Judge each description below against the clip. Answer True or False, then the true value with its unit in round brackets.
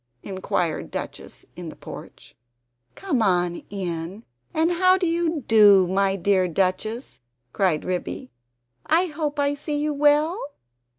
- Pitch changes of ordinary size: False (8.6 semitones)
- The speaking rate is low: True (125 wpm)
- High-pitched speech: True (225 Hz)